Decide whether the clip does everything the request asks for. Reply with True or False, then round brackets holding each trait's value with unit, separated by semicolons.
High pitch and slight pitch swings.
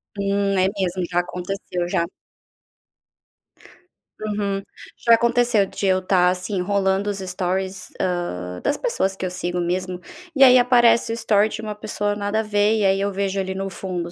True (195 Hz; 2.3 semitones)